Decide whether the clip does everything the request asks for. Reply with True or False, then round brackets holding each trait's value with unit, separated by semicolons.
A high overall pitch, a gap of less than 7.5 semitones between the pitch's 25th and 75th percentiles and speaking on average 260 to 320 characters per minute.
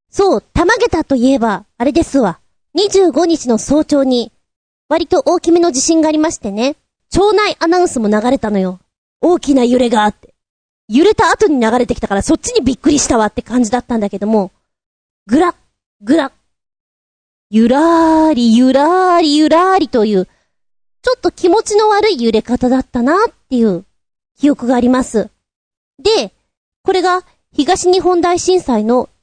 True (290 Hz; 6.5 semitones; 310 characters per minute)